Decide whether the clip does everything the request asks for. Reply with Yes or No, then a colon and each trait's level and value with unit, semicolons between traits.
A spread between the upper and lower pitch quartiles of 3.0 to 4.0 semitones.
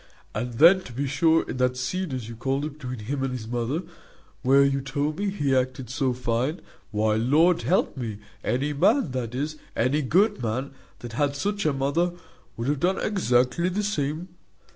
No: average, 4.4 semitones